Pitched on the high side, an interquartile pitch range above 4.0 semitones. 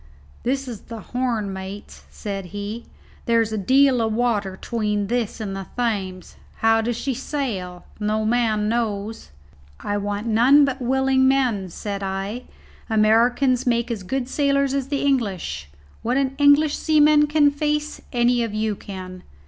Yes: high, 230 Hz; average, 4.4 semitones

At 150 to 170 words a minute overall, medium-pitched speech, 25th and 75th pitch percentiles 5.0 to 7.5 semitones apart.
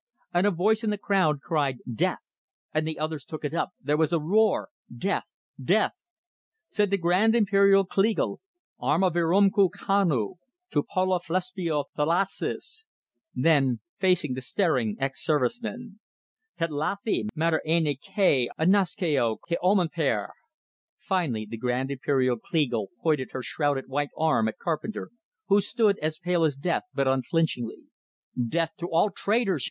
No: slow, 135 wpm; medium, 165 Hz; wide, 5.6 semitones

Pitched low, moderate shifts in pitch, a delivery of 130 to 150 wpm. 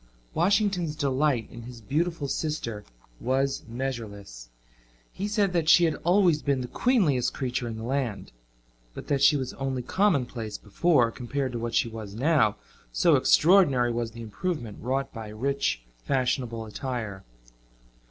Yes: low, 130 Hz; average, 4.9 semitones; average, 145 wpm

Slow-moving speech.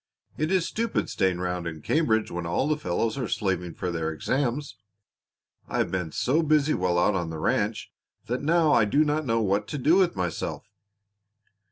No: average, 190 wpm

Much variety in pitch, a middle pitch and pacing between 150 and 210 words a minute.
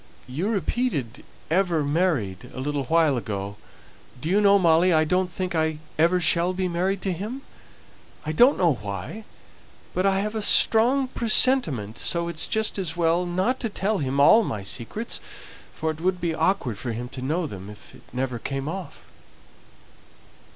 Yes: wide, 6.1 semitones; medium, 170 Hz; average, 170 wpm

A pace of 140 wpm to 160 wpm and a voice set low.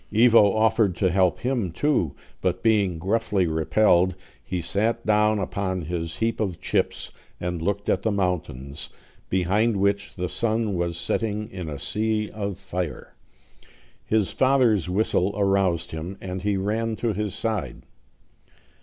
Yes: average, 145 wpm; low, 100 Hz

